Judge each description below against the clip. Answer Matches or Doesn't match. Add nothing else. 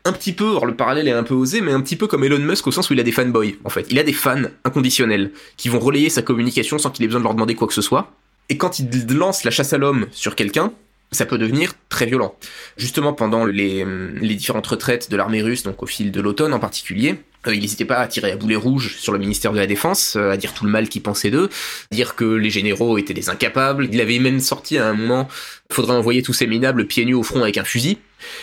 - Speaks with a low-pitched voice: Matches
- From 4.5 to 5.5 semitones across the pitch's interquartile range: Doesn't match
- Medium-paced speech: Doesn't match